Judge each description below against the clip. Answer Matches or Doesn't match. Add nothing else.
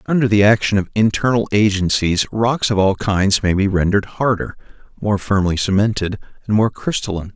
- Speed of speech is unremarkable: Matches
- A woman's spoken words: Doesn't match